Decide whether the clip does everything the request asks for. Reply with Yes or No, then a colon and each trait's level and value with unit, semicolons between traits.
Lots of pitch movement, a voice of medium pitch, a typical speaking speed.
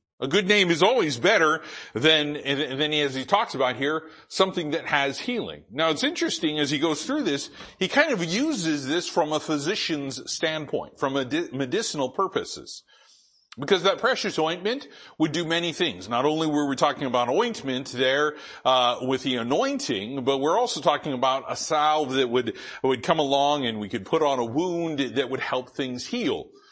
Yes: wide, 5.7 semitones; medium, 155 Hz; average, 190 wpm